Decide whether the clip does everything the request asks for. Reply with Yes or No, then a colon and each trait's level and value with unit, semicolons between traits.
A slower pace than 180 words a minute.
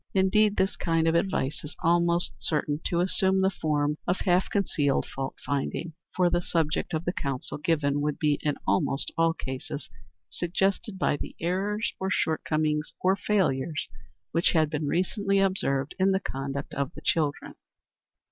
Yes: average, 160 wpm